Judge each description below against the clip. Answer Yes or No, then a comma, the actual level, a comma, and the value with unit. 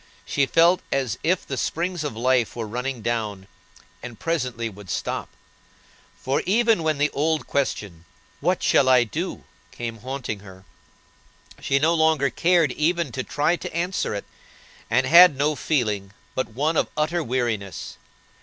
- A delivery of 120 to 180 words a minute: Yes, average, 155 wpm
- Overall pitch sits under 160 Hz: Yes, low, 135 Hz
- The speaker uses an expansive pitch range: Yes, wide, 5.7 semitones